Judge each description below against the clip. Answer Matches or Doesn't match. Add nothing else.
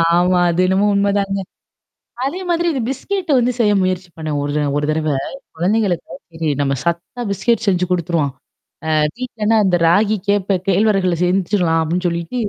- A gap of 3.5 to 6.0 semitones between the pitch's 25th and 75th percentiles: Matches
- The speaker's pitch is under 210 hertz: Matches